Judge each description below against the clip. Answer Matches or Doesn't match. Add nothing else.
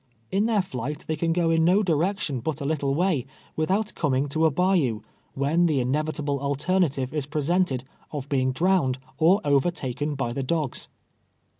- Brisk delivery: Doesn't match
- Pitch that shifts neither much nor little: Matches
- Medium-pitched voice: Matches